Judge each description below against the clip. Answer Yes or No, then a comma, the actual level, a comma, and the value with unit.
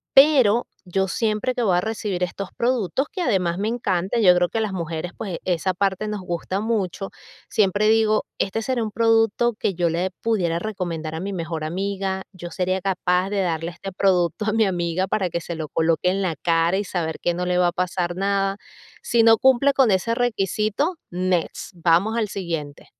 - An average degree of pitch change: Yes, average, 3.7 semitones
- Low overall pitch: No, high, 190 Hz